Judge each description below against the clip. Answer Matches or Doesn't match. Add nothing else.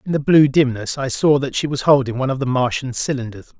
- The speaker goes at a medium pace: Doesn't match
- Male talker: Matches